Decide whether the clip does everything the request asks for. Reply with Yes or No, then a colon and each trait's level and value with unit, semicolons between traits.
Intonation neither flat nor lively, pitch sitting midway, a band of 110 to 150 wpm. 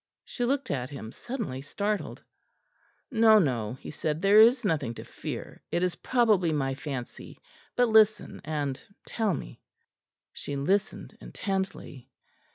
No: wide, 7.8 semitones; medium, 180 Hz; slow, 135 wpm